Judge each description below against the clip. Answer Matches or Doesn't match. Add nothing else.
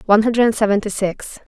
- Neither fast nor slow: Matches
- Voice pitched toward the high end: Matches